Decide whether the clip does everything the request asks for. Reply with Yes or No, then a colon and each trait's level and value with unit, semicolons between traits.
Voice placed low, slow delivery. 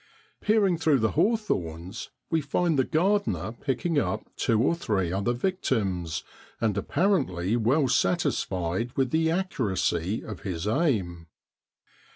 Yes: low, 120 Hz; slow, 130 wpm